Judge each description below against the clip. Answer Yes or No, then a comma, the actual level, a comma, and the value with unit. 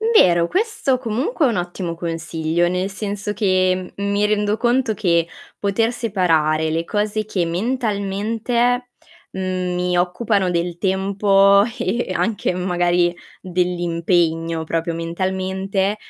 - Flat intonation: No, average, 3.4 semitones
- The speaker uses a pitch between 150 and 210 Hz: Yes, high, 190 Hz